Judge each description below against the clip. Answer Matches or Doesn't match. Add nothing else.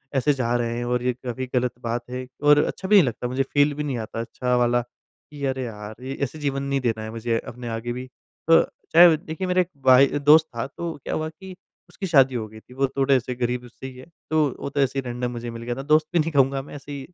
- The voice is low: Matches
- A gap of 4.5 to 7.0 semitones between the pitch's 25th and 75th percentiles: Doesn't match